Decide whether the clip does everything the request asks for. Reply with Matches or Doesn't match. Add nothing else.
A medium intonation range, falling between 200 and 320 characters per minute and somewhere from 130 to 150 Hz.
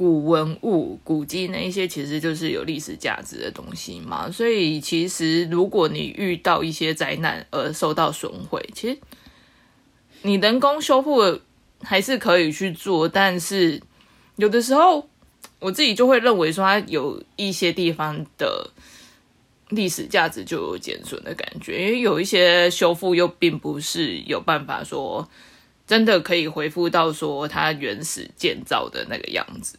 Doesn't match